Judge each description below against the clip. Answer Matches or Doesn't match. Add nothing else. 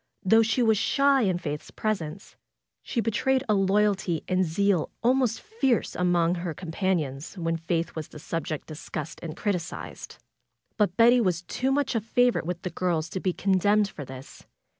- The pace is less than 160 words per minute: Doesn't match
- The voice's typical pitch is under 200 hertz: Matches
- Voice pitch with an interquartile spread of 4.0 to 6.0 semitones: Matches